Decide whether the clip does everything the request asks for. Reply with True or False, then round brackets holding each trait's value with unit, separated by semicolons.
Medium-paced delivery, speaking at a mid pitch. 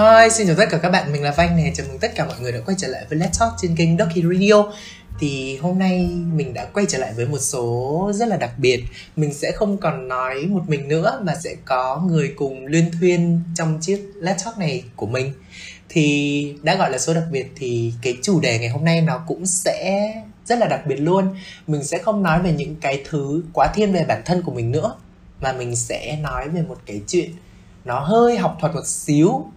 True (235 wpm; 160 Hz)